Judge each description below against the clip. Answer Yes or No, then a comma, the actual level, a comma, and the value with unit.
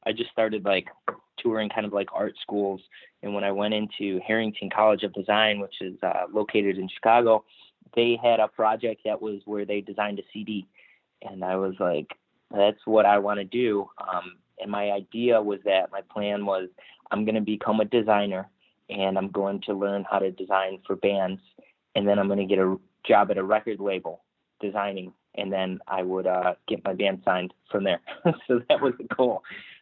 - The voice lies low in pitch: Yes, low, 100 Hz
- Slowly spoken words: No, average, 200 wpm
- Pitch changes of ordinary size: No, narrow, 1.7 semitones